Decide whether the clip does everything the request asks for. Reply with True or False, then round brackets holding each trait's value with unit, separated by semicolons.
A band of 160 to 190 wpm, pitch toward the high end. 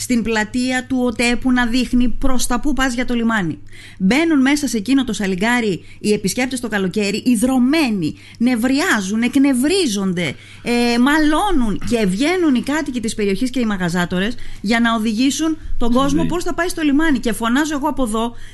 True (170 wpm; 245 Hz)